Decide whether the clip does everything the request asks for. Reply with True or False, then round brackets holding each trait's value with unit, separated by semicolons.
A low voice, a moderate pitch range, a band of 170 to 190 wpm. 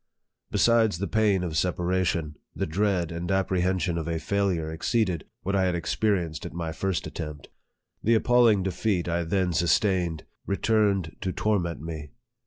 False (90 Hz; 3.1 semitones; 155 wpm)